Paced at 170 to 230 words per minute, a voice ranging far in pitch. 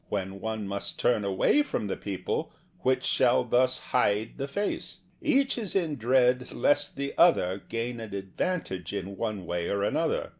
Yes: average, 175 wpm; wide, 5.8 semitones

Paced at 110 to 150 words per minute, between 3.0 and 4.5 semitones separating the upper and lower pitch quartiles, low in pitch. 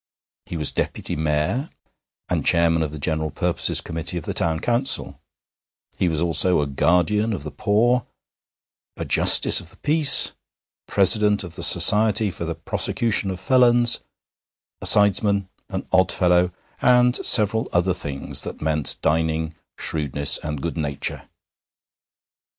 No: average, 140 wpm; average, 5.0 semitones; very low, 90 Hz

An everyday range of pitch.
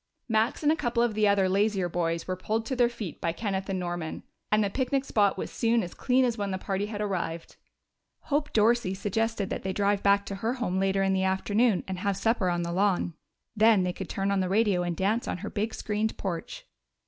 Yes: average, 3.1 semitones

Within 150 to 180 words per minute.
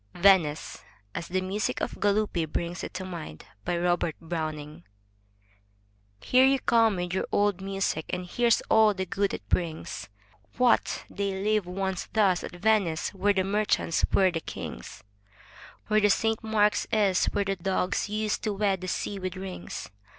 Yes: average, 160 wpm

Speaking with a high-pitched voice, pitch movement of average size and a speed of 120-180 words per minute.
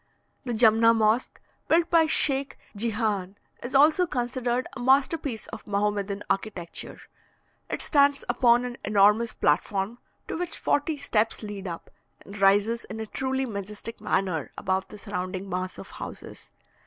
Yes: high, 225 Hz; average, 4.4 semitones; average, 145 wpm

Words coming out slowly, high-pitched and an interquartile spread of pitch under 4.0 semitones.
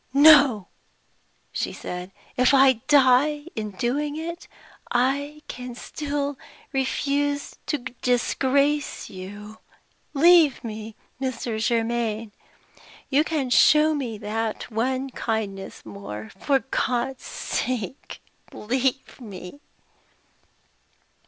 No: slow, 95 wpm; very high, 255 Hz; average, 4.4 semitones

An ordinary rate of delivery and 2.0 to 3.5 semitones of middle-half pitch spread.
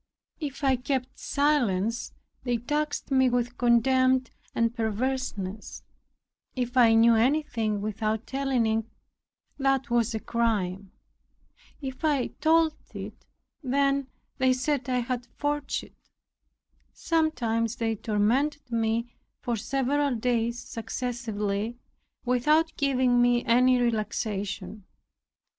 No: slow, 110 wpm; average, 3.1 semitones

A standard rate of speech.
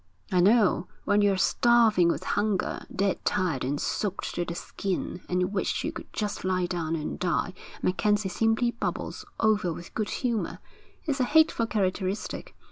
Yes: average, 160 wpm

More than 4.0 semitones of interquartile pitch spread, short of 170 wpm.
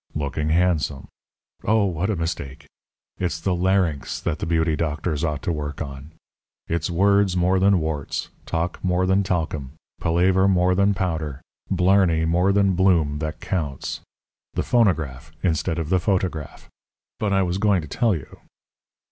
No: average, 3.4 semitones; average, 155 wpm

